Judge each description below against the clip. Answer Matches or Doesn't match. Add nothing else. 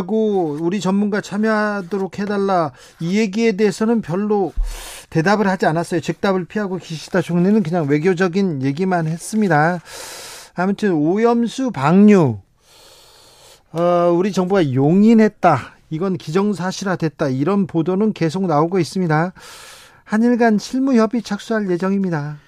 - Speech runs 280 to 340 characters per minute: Matches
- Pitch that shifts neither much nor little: Matches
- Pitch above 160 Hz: Matches